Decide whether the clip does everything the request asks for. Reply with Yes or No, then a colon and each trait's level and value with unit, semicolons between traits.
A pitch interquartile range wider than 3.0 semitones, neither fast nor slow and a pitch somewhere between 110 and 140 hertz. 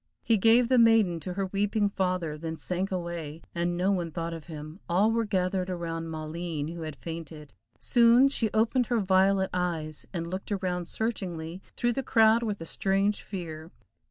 No: average, 4.0 semitones; average, 180 wpm; medium, 185 Hz